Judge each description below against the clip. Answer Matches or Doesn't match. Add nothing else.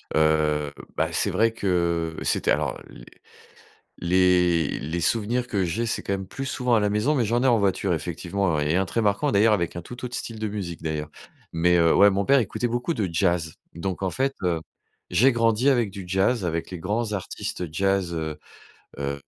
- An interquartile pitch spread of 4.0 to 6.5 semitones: Matches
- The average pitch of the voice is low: Matches